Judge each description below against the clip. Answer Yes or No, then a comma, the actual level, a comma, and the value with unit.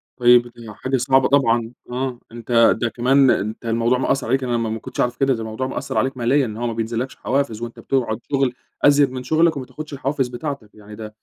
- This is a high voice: No, low, 125 Hz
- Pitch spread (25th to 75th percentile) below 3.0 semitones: Yes, narrow, 2.6 semitones